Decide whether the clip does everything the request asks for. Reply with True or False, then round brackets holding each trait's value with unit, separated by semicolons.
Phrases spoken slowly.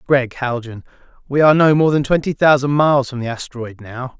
False (200 wpm)